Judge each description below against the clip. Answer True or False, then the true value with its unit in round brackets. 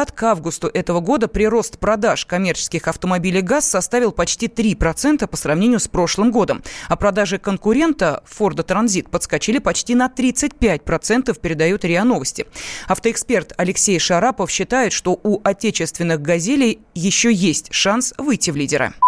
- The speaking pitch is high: True (200 Hz)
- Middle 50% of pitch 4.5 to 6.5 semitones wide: True (5.1 semitones)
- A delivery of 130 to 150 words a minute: True (140 wpm)